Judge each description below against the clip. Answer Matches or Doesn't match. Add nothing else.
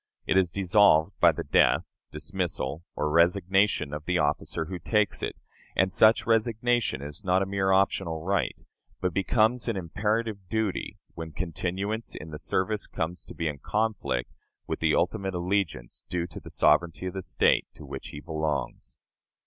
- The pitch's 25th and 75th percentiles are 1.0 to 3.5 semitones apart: Doesn't match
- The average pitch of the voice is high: Doesn't match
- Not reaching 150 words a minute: Doesn't match